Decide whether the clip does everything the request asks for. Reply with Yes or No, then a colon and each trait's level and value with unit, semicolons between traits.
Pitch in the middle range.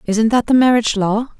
No: high, 225 Hz